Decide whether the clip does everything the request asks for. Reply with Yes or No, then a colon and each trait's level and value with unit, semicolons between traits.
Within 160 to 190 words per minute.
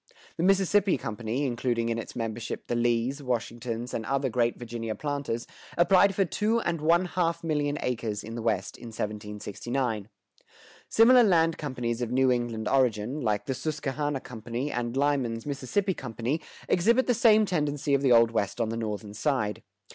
Yes: average, 165 wpm